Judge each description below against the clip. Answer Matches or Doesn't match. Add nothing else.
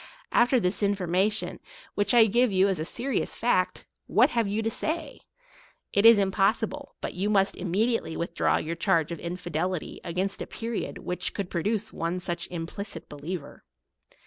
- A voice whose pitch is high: Matches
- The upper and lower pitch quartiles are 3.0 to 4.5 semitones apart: Matches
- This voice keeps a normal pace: Matches